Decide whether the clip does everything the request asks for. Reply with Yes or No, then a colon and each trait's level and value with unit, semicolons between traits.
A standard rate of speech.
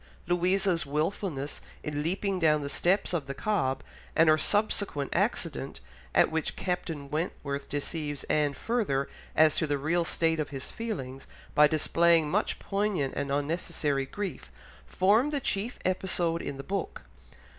Yes: average, 145 wpm